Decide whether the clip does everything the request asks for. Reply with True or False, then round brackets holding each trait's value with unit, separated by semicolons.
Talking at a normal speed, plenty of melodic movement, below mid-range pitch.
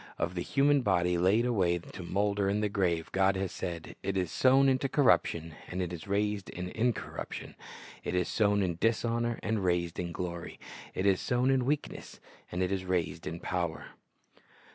False (180 wpm; 4.2 semitones; 95 Hz)